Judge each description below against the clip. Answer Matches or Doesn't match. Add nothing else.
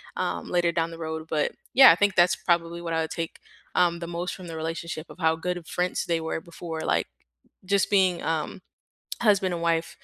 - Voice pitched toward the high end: Doesn't match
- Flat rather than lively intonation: Matches